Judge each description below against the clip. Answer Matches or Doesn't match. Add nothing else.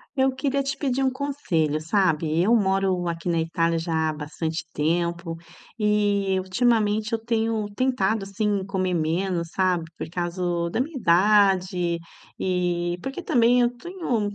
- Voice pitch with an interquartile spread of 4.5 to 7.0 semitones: Matches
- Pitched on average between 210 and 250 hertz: Doesn't match